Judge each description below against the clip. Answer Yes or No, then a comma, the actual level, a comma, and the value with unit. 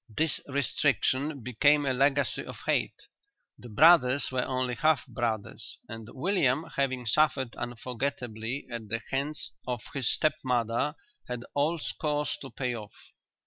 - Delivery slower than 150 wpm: Yes, average, 140 wpm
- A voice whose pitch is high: No, low, 130 Hz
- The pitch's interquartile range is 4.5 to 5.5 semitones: No, average, 3.3 semitones